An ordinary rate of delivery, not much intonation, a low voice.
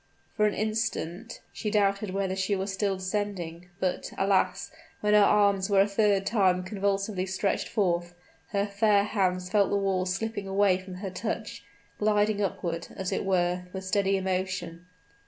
No: average, 160 wpm; narrow, 1.8 semitones; high, 195 Hz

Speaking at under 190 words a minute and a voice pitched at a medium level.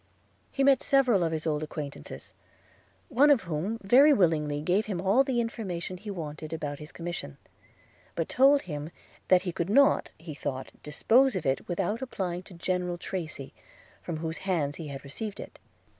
Yes: average, 175 wpm; medium, 175 Hz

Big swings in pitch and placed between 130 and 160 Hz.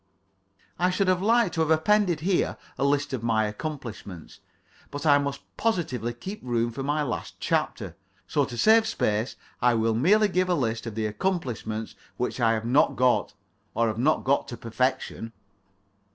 Yes: wide, 7.2 semitones; low, 135 Hz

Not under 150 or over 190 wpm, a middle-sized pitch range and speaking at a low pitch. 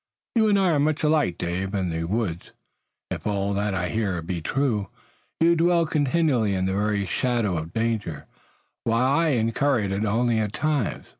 No: average, 175 wpm; wide, 6.8 semitones; low, 110 Hz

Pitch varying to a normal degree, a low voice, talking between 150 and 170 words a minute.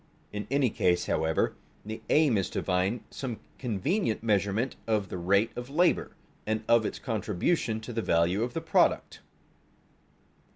Yes: average, 3.8 semitones; low, 110 Hz; average, 155 wpm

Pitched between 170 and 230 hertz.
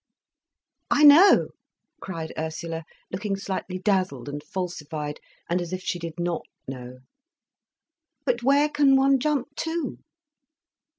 Yes: medium, 185 Hz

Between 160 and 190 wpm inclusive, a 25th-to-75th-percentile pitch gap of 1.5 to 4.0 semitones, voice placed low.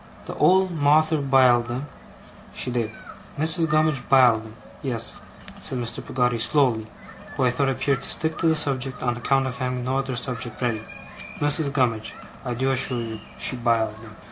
Yes: average, 175 wpm; average, 2.8 semitones; low, 130 Hz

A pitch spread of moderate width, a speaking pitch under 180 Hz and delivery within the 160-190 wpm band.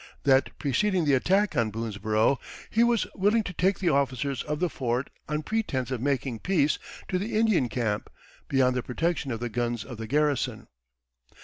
No: wide, 7.0 semitones; medium, 140 Hz; average, 180 wpm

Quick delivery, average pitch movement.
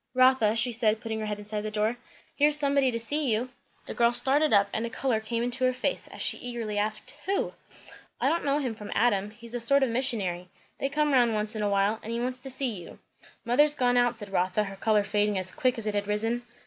Yes: fast, 250 wpm; average, 3.4 semitones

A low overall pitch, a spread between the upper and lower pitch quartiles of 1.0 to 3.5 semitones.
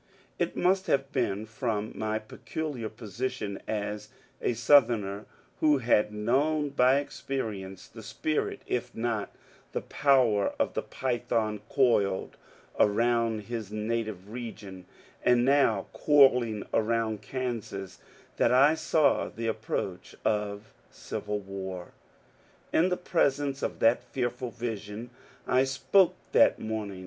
No: low, 115 Hz; average, 4.0 semitones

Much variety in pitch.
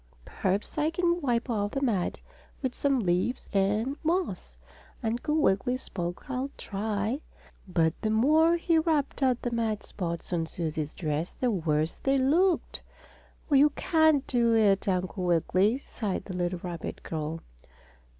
Yes: wide, 7.4 semitones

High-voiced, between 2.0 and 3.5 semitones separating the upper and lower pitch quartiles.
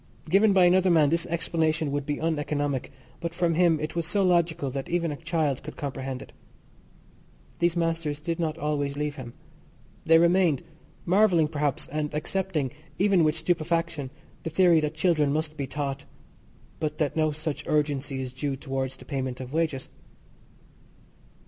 No: medium, 155 Hz; average, 2.8 semitones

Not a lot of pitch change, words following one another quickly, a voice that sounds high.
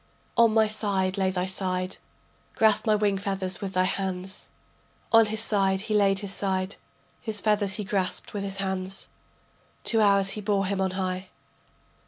No: narrow, 1.8 semitones; average, 170 wpm; high, 195 Hz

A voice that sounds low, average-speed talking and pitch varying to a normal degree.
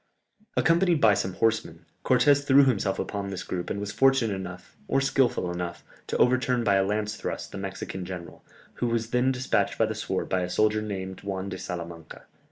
Yes: low, 100 Hz; average, 190 wpm; average, 4.9 semitones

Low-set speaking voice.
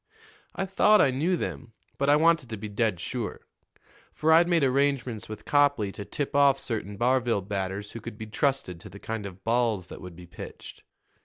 Yes: low, 115 Hz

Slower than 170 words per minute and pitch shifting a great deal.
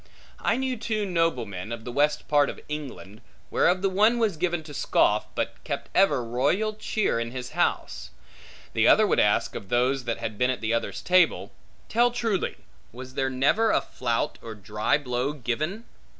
No: average, 180 wpm; wide, 8.1 semitones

